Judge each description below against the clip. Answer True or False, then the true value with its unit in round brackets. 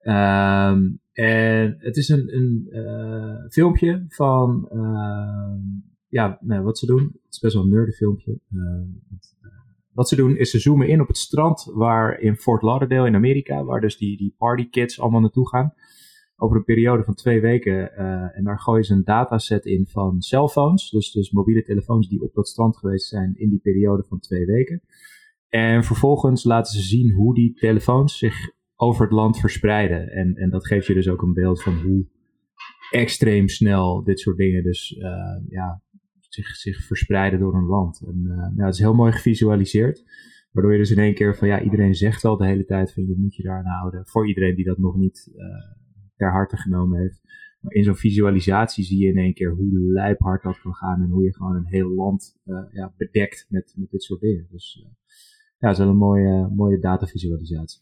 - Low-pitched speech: True (100 Hz)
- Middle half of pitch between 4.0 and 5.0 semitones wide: False (3.2 semitones)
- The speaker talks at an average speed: False (205 wpm)